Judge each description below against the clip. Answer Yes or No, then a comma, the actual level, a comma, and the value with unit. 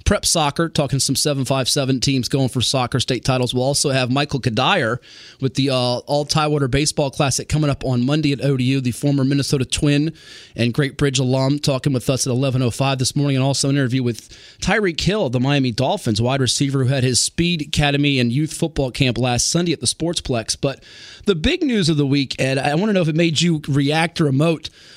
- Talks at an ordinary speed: No, fast, 210 wpm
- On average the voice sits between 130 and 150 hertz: Yes, medium, 140 Hz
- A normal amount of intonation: No, narrow, 2.3 semitones